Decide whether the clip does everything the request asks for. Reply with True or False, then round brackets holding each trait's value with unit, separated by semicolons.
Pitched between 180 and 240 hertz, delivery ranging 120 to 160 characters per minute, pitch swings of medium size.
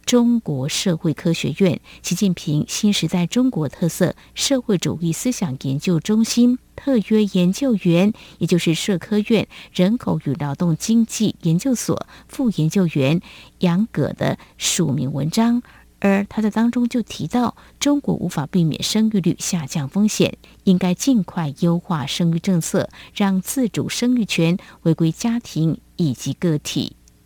False (185 Hz; 230 characters per minute; 5.0 semitones)